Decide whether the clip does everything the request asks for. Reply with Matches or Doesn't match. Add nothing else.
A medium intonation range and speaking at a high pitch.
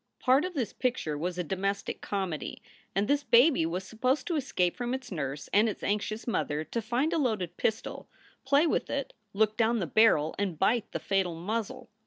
Doesn't match